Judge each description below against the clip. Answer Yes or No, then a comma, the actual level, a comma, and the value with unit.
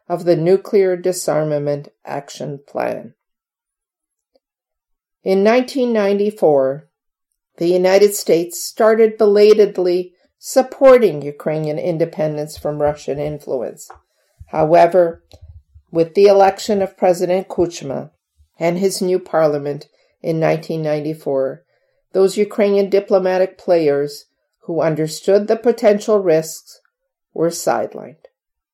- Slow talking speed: Yes, slow, 90 wpm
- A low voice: No, medium, 180 Hz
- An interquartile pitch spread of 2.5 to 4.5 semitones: No, average, 4.9 semitones